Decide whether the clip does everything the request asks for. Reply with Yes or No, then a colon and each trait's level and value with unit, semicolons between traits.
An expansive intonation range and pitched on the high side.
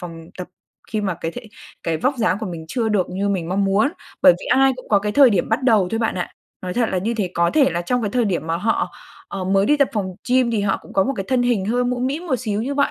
No: average, 5.0 semitones; high, 210 Hz